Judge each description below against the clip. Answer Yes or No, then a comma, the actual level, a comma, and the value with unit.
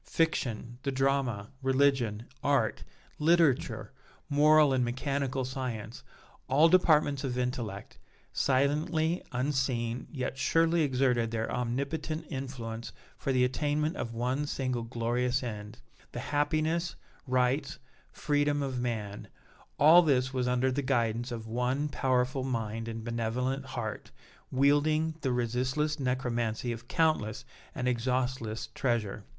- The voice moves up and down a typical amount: Yes, average, 3.3 semitones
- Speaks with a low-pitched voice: Yes, low, 130 Hz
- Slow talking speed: Yes, slow, 120 wpm